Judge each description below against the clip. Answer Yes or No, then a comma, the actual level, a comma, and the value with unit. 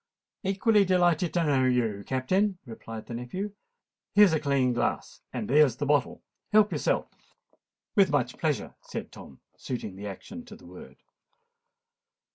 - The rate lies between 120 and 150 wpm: Yes, average, 140 wpm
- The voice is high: No, medium, 145 Hz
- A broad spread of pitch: Yes, wide, 7.3 semitones